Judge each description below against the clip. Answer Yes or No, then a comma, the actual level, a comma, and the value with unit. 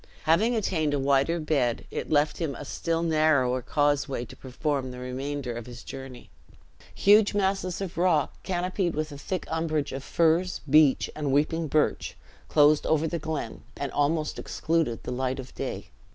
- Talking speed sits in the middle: Yes, average, 165 wpm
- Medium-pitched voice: Yes, medium, 150 Hz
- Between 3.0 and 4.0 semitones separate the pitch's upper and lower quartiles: Yes, average, 3.5 semitones